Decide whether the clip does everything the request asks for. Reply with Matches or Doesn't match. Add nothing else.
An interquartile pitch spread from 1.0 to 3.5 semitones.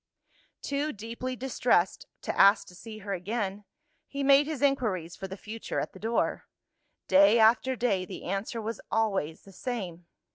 Doesn't match